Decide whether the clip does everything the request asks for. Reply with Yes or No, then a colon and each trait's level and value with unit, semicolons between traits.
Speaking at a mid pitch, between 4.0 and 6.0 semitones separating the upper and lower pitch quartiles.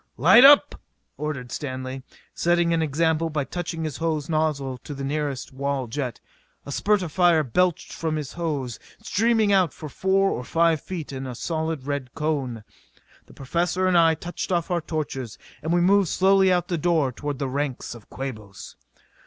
Yes: medium, 155 Hz; average, 4.3 semitones